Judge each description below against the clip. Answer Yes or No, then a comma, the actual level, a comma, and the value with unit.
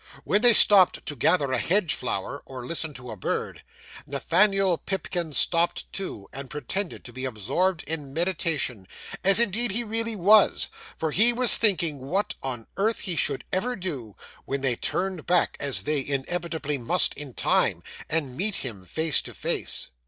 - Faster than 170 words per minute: No, average, 165 wpm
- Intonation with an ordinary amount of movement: No, wide, 6.3 semitones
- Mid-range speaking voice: Yes, medium, 165 Hz